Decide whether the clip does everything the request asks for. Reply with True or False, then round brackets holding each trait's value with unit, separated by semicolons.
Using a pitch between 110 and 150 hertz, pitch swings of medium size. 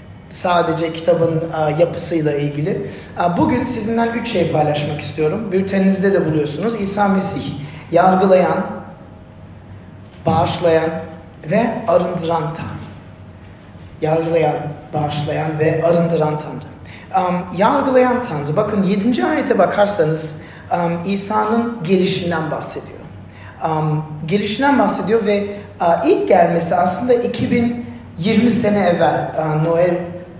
False (170 Hz; 4.9 semitones)